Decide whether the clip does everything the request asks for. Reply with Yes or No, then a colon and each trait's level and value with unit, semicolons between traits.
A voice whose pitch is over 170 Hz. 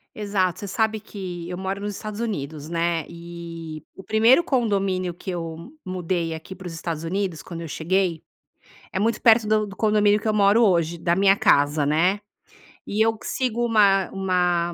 Yes: high, 190 Hz